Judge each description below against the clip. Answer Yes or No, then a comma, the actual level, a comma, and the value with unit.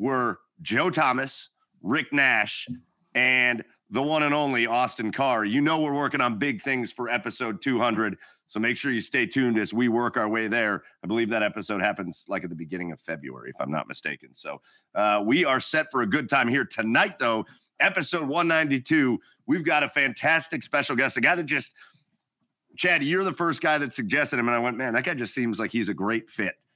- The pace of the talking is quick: Yes, fast, 210 wpm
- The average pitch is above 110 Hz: Yes, low, 120 Hz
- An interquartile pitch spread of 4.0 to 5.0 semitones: Yes, average, 4.6 semitones